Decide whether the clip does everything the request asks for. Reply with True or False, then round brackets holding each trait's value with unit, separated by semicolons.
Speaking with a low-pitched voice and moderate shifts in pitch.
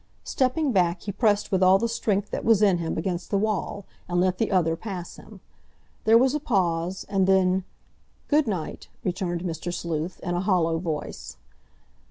False (185 Hz; 3.2 semitones)